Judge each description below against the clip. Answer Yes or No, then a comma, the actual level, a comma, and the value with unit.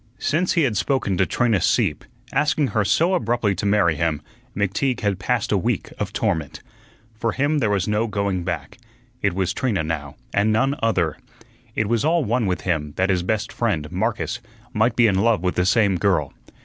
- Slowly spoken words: No, average, 195 wpm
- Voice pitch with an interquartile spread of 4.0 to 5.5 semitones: Yes, average, 4.5 semitones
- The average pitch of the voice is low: Yes, low, 105 Hz